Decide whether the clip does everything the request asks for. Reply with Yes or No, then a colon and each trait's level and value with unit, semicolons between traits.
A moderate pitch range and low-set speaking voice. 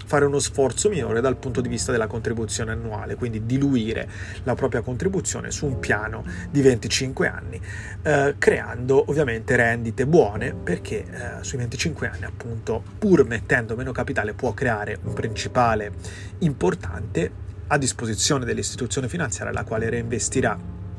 Yes: average, 3.9 semitones; low, 115 Hz